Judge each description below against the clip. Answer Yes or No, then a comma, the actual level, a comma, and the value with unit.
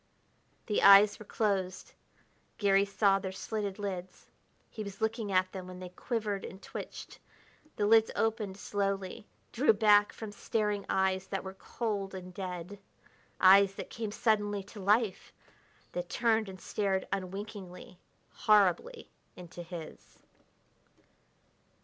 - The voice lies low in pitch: No, high, 200 Hz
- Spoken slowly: Yes, slow, 130 wpm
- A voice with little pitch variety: Yes, narrow, 2.0 semitones